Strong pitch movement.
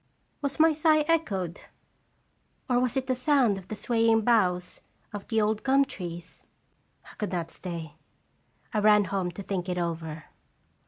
Yes: wide, 6.1 semitones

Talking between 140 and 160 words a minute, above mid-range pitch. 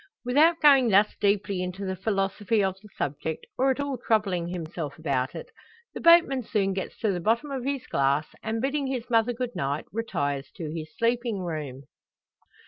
No: average, 180 wpm; high, 205 Hz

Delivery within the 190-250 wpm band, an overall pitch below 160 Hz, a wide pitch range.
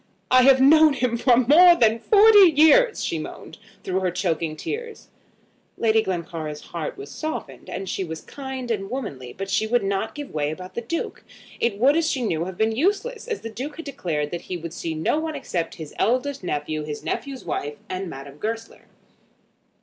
No: average, 195 wpm; high, 220 Hz; wide, 8.8 semitones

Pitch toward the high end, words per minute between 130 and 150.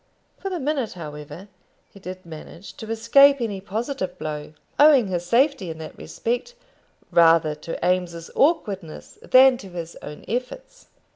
Yes: high, 195 Hz; average, 145 wpm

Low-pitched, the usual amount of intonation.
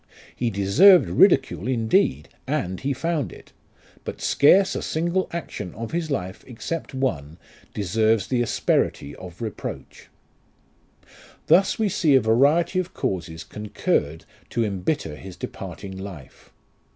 No: low, 115 Hz; wide, 8.9 semitones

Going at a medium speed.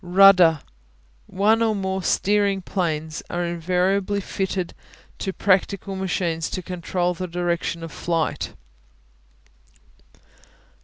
No: slow, 100 wpm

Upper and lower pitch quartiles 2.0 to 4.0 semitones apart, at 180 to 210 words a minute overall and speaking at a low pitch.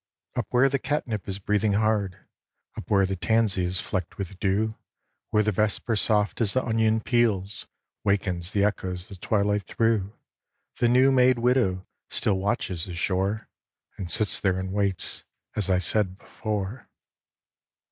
No: average, 2.8 semitones; average, 155 wpm; low, 105 Hz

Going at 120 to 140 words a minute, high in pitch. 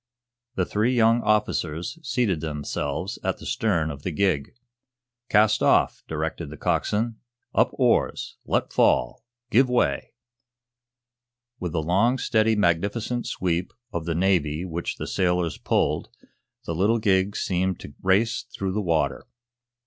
No: slow, 135 wpm; very low, 95 Hz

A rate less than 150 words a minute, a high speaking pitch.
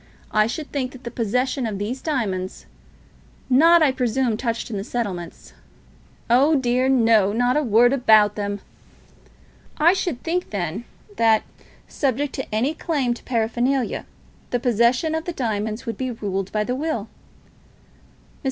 No: average, 160 wpm; high, 240 Hz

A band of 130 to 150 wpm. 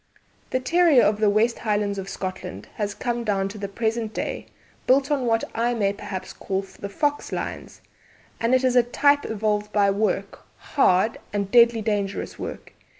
No: average, 175 wpm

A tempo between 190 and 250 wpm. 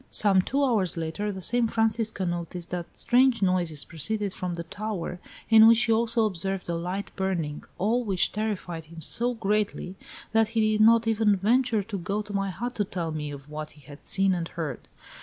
Yes: average, 195 wpm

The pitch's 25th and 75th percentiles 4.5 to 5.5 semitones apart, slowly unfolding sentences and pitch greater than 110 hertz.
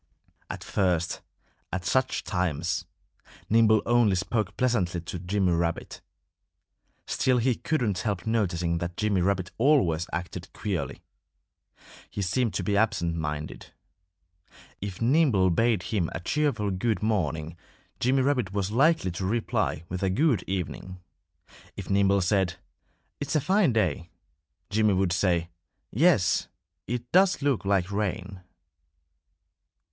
No: average, 4.9 semitones; slow, 125 wpm; low, 100 Hz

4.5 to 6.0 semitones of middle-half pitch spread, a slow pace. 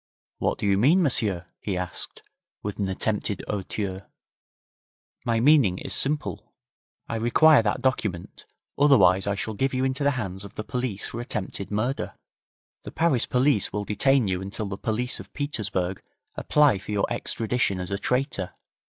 No: average, 5.0 semitones; average, 160 wpm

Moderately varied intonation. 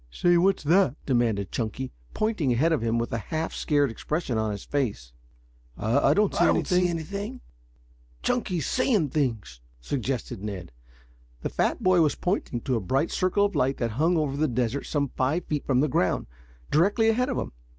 No: wide, 7.2 semitones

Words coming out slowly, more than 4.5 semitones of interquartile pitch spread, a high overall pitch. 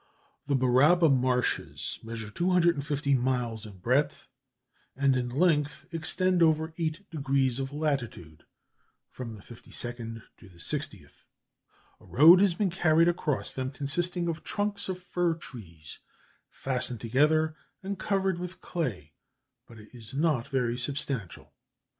No: slow, 130 wpm; wide, 5.5 semitones; medium, 140 Hz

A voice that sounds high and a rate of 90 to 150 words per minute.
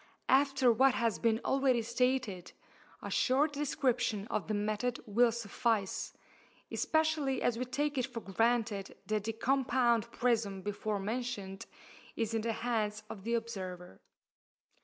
Yes: high, 230 Hz; average, 140 wpm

